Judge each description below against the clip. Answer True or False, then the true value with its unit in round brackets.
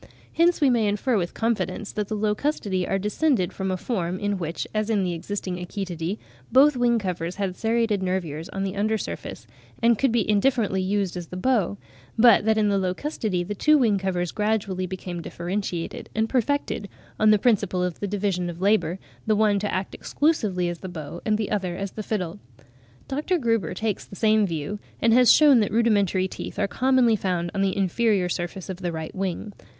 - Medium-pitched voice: False (200 Hz)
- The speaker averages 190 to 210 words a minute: True (195 wpm)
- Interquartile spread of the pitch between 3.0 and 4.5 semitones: True (3.4 semitones)